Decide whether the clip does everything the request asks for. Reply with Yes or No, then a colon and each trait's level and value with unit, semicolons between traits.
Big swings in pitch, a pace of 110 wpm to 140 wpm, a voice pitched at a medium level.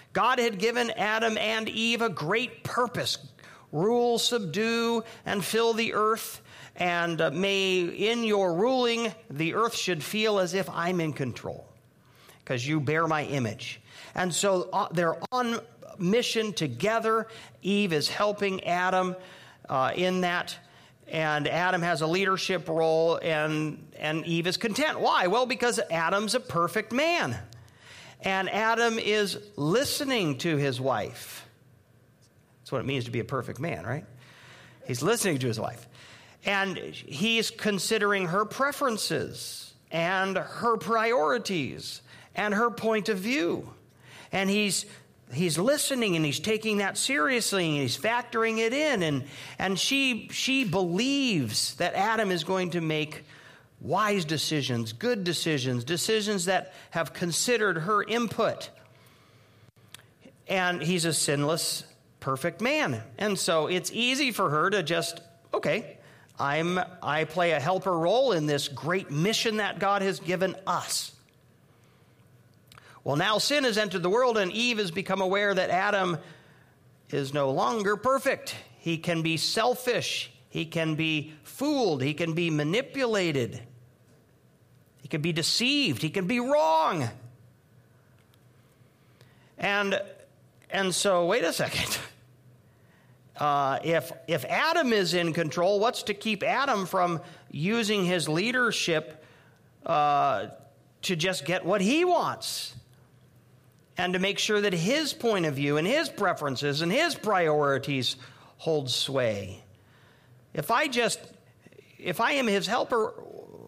Yes: wide, 7.5 semitones; slow, 135 wpm; medium, 175 Hz